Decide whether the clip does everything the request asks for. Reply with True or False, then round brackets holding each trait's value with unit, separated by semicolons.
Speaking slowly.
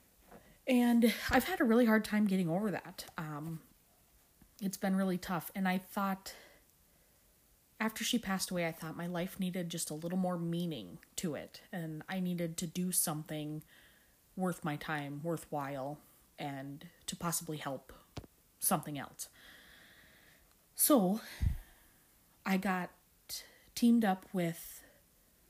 True (130 wpm)